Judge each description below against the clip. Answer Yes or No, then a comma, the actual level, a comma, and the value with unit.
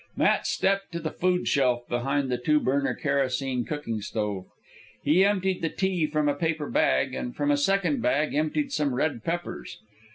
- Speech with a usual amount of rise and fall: Yes, average, 4.8 semitones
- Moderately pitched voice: Yes, medium, 145 Hz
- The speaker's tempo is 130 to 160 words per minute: No, average, 175 wpm